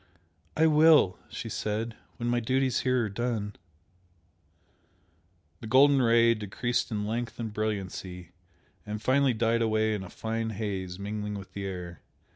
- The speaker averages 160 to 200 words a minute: No, average, 145 wpm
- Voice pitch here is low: Yes, low, 110 Hz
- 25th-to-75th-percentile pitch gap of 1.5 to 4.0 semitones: Yes, average, 2.8 semitones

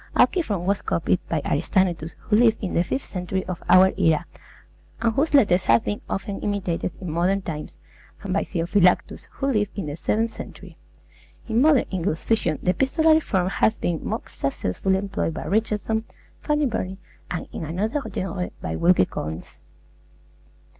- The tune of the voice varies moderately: Yes, average, 4.2 semitones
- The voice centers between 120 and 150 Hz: No, high, 190 Hz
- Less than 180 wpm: Yes, average, 160 wpm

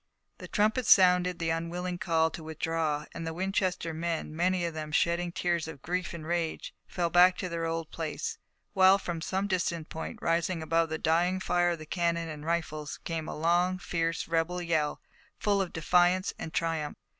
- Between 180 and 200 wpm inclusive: Yes, average, 185 wpm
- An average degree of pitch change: No, narrow, 1.7 semitones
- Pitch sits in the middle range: Yes, medium, 170 Hz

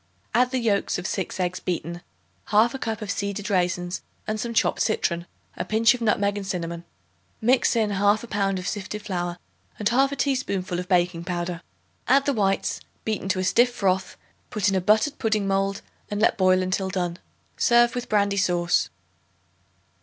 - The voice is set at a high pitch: Yes, high, 200 Hz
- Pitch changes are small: No, average, 3.3 semitones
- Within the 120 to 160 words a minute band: No, average, 175 wpm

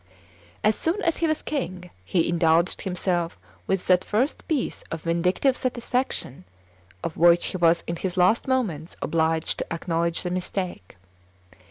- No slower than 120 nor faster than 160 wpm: Yes, average, 150 wpm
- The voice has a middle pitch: Yes, medium, 180 Hz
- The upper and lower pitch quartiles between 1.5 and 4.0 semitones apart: No, average, 4.7 semitones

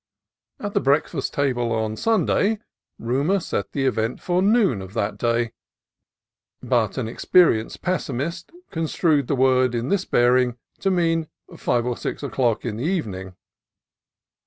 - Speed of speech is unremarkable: Yes, average, 145 wpm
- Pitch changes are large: Yes, wide, 6.2 semitones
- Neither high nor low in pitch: No, low, 130 Hz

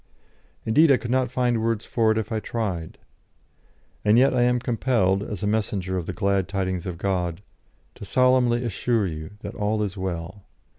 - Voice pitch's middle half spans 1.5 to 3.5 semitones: No, average, 4.2 semitones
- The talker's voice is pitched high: No, low, 105 Hz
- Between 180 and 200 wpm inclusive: Yes, average, 185 wpm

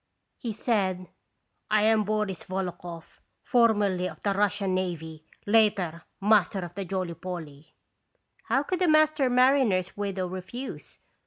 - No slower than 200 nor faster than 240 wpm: No, slow, 135 wpm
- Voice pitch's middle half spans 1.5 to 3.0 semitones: No, average, 3.5 semitones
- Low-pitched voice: No, high, 195 Hz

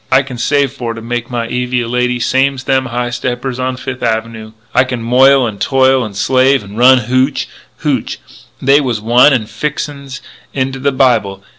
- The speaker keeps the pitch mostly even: Yes, narrow, 2.0 semitones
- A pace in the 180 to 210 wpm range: Yes, average, 185 wpm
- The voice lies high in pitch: No, low, 125 Hz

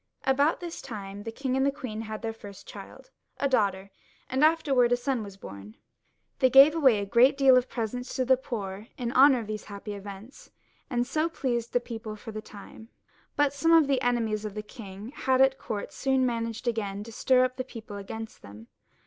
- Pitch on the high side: Yes, high, 235 Hz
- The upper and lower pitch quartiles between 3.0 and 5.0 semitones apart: Yes, average, 3.9 semitones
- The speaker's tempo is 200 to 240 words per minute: Yes, fast, 205 wpm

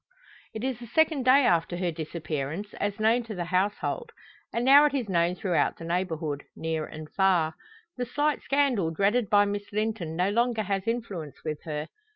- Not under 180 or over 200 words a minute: Yes, average, 185 wpm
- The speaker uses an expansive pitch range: Yes, wide, 6.1 semitones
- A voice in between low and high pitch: No, high, 200 Hz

